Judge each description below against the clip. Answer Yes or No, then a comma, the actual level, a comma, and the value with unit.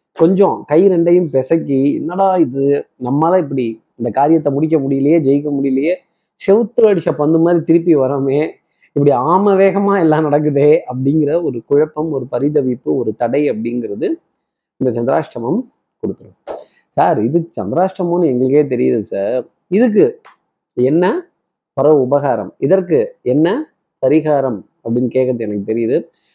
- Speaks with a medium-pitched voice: Yes, medium, 150 Hz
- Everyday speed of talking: Yes, average, 120 wpm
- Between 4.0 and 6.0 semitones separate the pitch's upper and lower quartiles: Yes, average, 4.8 semitones